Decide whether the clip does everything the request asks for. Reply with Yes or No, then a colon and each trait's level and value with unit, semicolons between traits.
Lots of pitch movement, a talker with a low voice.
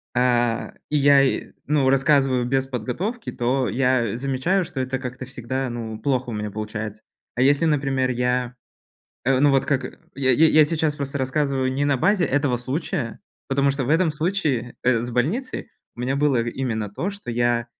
No: average, 2.8 semitones; low, 130 Hz